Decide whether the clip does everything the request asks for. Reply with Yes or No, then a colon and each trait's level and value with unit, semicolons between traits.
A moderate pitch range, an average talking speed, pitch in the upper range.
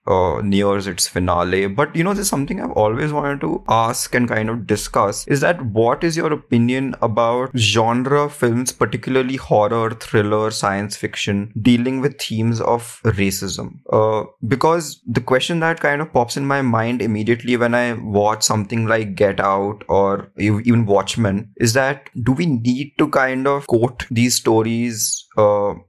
No: average, 3.7 semitones; average, 165 wpm; low, 120 Hz